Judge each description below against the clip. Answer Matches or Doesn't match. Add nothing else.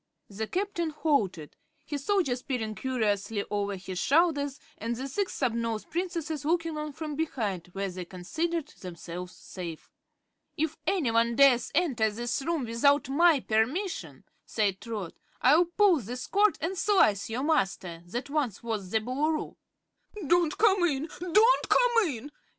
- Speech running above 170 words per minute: Doesn't match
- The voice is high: Matches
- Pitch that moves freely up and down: Matches